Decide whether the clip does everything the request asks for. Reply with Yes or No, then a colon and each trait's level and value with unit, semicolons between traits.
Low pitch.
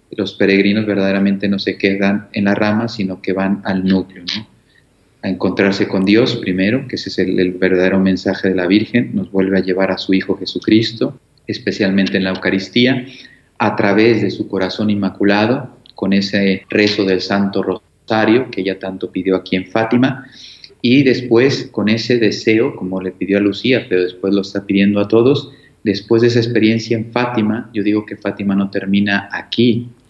Yes: low, 100 Hz